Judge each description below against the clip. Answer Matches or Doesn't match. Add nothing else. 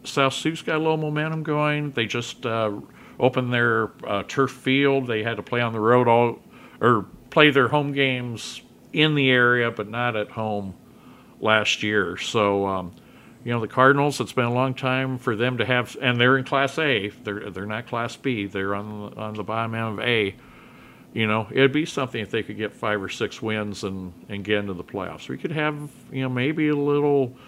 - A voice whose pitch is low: Matches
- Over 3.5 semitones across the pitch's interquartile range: Matches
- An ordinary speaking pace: Doesn't match